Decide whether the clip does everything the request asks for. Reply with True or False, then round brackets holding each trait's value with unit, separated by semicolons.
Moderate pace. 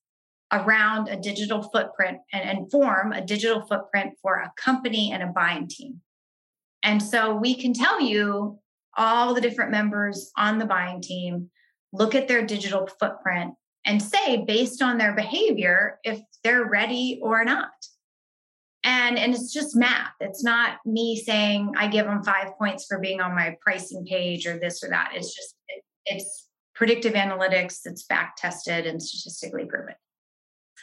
True (160 wpm)